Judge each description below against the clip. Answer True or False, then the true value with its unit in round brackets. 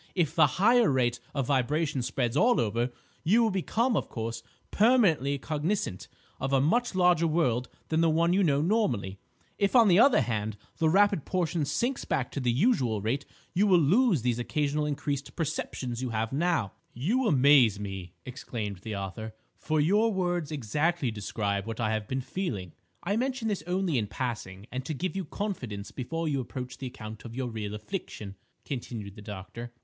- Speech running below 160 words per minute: False (180 wpm)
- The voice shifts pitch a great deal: True (7.5 semitones)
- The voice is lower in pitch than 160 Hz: True (140 Hz)